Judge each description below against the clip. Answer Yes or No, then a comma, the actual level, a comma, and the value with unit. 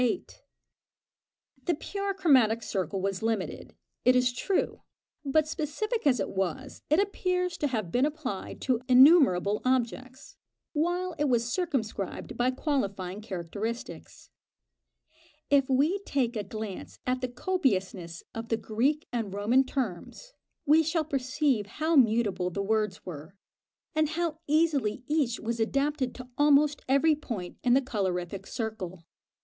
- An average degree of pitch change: No, wide, 6.1 semitones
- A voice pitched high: Yes, very high, 255 Hz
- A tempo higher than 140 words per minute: No, slow, 135 wpm